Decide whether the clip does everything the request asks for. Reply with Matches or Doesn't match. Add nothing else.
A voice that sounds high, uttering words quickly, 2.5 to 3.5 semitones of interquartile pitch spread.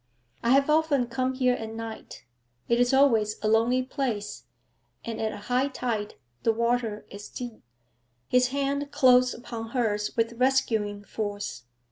Doesn't match